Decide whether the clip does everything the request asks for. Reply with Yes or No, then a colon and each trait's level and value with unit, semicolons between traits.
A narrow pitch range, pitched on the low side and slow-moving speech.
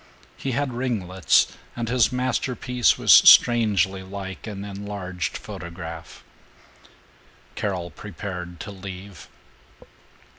No: average, 4.3 semitones; low, 100 Hz; slow, 90 wpm